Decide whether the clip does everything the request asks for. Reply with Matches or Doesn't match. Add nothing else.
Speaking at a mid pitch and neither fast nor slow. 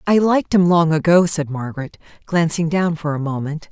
Matches